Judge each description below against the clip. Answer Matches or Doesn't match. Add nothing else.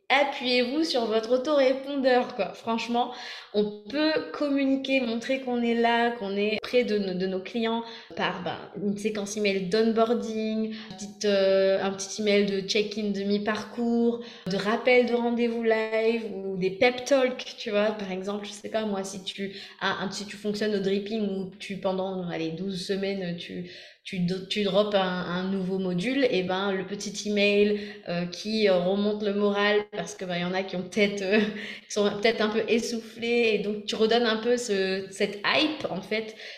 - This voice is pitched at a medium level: Doesn't match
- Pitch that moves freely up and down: Doesn't match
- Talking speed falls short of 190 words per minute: Matches